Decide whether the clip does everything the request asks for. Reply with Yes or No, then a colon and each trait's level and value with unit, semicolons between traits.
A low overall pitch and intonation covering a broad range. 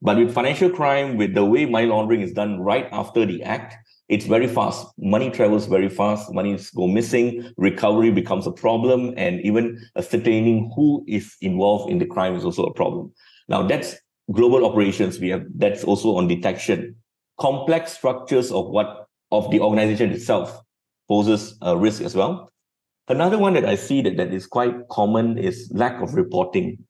No: low, 115 Hz; average, 2.7 semitones